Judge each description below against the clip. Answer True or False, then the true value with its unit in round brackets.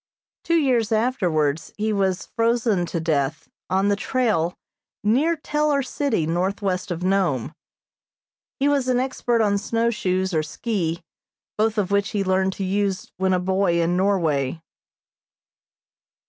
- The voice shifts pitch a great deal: False (4.6 semitones)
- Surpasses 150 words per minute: False (135 wpm)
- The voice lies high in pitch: True (195 Hz)